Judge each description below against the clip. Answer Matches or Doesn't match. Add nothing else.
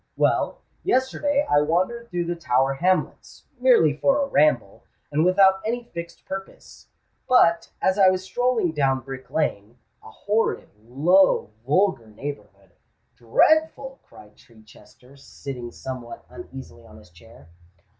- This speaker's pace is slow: Matches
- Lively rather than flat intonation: Matches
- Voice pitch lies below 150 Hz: Doesn't match